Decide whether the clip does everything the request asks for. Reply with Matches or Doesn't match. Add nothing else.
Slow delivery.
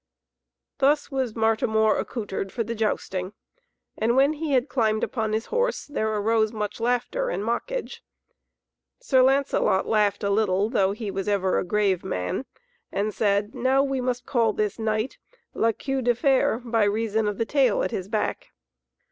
Doesn't match